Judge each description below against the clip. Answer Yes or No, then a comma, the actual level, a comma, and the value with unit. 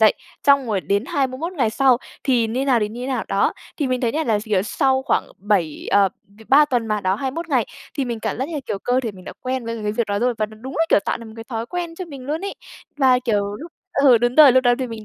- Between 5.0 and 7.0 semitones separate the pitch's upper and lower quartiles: No, average, 3.9 semitones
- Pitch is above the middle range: Yes, high, 245 Hz